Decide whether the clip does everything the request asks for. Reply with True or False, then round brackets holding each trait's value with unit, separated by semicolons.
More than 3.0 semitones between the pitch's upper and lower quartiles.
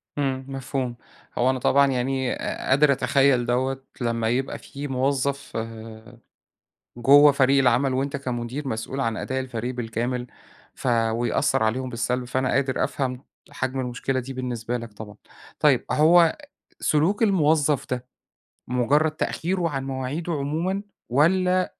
False (2.5 semitones)